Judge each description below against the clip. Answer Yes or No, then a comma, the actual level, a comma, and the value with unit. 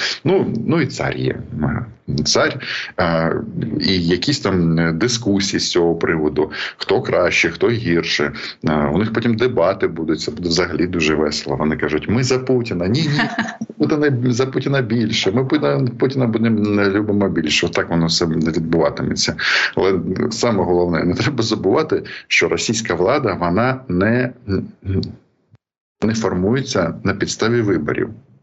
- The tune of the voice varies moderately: No, wide, 6.9 semitones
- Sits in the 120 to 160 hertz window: No, low, 100 Hz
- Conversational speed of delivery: Yes, average, 135 wpm